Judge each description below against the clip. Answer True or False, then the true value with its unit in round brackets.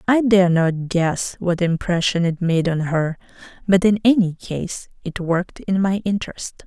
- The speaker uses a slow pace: False (170 wpm)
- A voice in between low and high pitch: True (180 Hz)